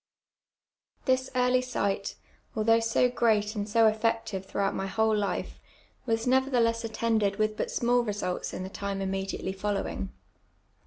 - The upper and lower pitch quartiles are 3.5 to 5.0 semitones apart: No, average, 2.7 semitones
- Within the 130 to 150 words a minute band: Yes, average, 145 wpm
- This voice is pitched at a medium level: No, high, 220 Hz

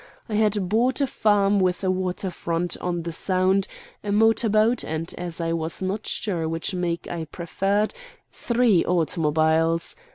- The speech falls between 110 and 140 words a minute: No, average, 155 wpm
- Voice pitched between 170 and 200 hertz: Yes, medium, 185 Hz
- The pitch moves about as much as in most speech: Yes, average, 3.8 semitones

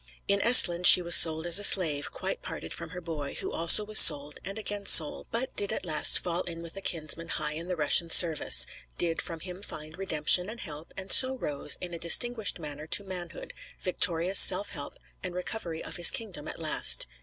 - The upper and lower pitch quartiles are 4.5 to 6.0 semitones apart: No, average, 3.3 semitones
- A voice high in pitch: No, medium, 175 Hz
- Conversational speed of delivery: No, fast, 210 wpm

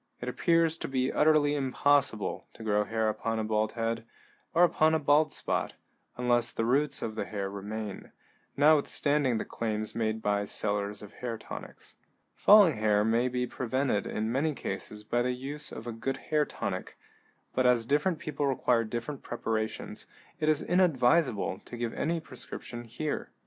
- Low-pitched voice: Yes, low, 120 Hz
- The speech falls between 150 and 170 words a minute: Yes, average, 165 wpm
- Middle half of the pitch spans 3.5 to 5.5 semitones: Yes, average, 4.9 semitones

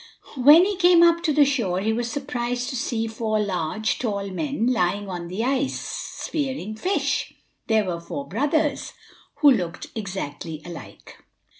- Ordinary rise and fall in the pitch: No, wide, 6.3 semitones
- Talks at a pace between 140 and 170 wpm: Yes, average, 155 wpm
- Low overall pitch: No, high, 230 Hz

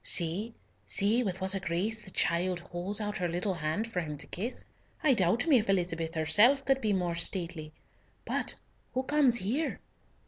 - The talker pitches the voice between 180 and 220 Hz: Yes, high, 190 Hz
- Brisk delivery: No, average, 180 wpm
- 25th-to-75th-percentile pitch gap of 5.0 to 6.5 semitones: No, average, 4.6 semitones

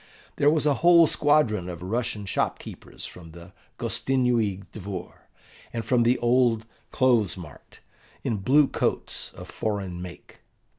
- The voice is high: No, low, 115 Hz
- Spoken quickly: No, average, 140 wpm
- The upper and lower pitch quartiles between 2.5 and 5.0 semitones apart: No, wide, 5.6 semitones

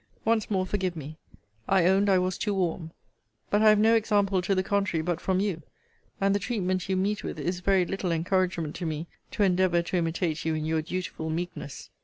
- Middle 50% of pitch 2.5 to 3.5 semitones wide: Yes, average, 2.8 semitones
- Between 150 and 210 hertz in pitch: Yes, medium, 185 Hz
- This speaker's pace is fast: Yes, fast, 210 wpm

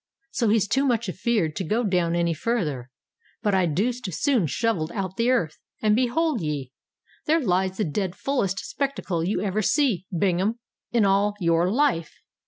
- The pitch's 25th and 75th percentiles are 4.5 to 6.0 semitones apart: Yes, wide, 5.4 semitones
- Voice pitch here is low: No, high, 200 Hz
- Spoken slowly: No, average, 165 wpm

